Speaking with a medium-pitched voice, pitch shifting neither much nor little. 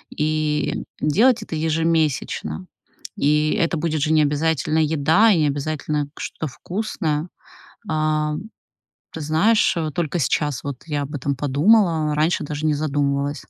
No: medium, 155 Hz; narrow, 1.8 semitones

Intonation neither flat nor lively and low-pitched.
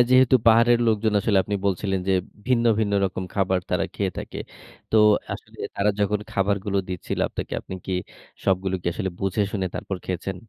No: narrow, 2.3 semitones; low, 100 Hz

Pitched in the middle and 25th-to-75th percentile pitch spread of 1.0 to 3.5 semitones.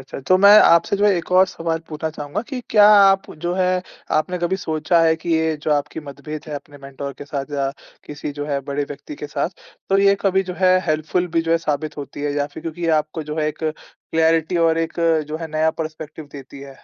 Yes: medium, 160 Hz; average, 3.2 semitones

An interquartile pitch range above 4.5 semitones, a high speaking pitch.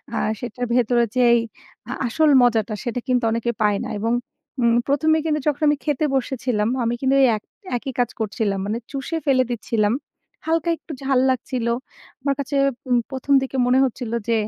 No: average, 3.0 semitones; very high, 250 Hz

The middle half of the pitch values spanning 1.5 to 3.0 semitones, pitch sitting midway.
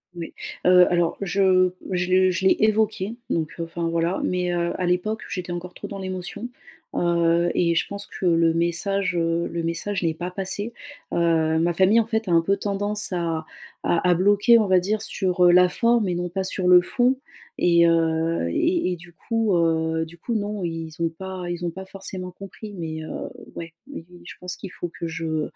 Yes: average, 2.7 semitones; medium, 180 Hz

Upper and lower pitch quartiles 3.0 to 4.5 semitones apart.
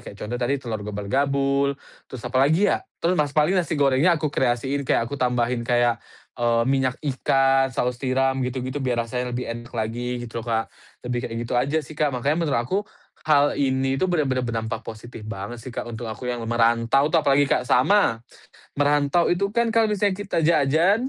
Yes: average, 3.4 semitones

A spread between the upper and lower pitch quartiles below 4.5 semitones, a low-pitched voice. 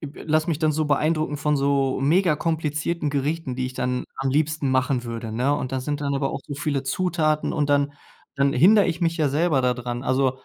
No: average, 2.8 semitones; medium, 145 Hz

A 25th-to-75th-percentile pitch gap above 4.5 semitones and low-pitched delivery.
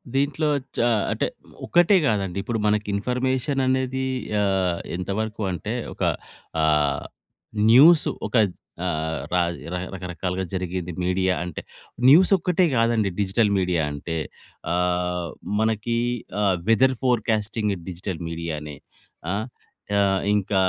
Yes: average, 5.1 semitones; low, 100 Hz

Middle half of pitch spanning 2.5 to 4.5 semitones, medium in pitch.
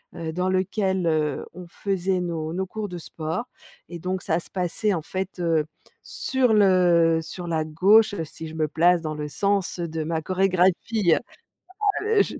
Yes: average, 2.9 semitones; medium, 180 Hz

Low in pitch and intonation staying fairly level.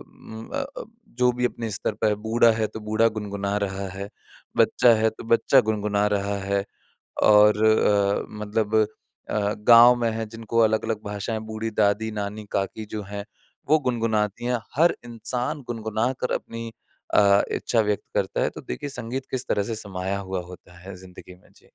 Yes: low, 110 Hz; narrow, 2.2 semitones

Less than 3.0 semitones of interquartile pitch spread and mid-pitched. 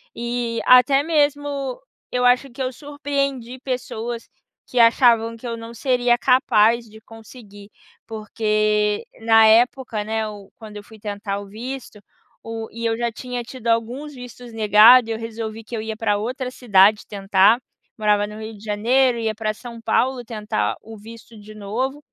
No: narrow, 2.6 semitones; high, 230 Hz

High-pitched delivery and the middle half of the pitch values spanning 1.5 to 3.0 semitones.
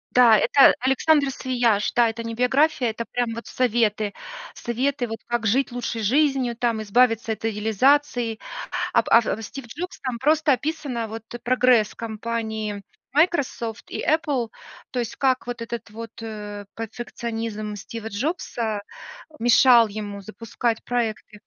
Yes: high, 235 Hz; narrow, 2.5 semitones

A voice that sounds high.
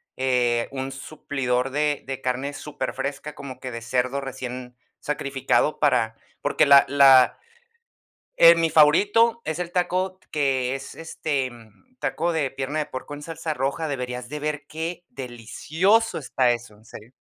No: medium, 140 Hz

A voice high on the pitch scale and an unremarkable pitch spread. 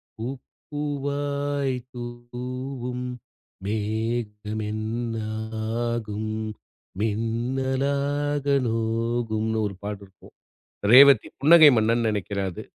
No: low, 120 Hz; average, 3.9 semitones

